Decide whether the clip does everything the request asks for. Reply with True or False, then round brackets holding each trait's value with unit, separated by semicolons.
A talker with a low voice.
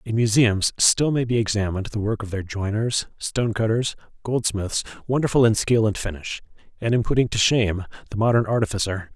True (110 Hz)